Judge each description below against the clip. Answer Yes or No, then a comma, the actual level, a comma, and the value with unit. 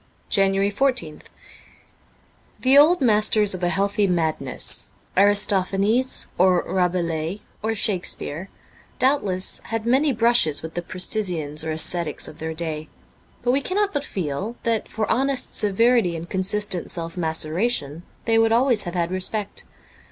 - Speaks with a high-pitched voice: Yes, high, 195 Hz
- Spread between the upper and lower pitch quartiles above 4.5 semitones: Yes, average, 5.0 semitones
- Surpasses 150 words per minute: No, average, 145 wpm